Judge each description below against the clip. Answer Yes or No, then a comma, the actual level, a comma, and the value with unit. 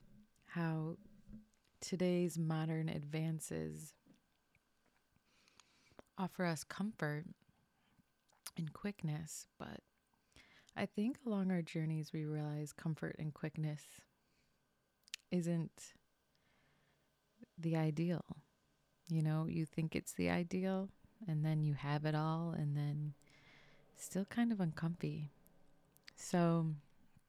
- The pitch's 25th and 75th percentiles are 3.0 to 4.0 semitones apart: Yes, average, 3.4 semitones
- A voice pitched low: No, medium, 160 Hz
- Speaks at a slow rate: Yes, slow, 95 wpm